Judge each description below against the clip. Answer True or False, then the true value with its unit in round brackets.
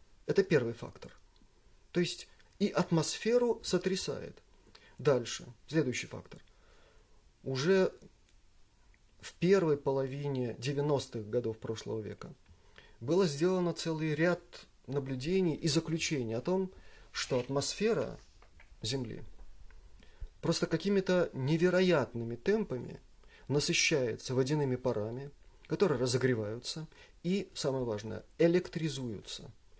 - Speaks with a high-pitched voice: False (140 Hz)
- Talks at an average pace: False (90 wpm)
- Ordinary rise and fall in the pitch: False (6.9 semitones)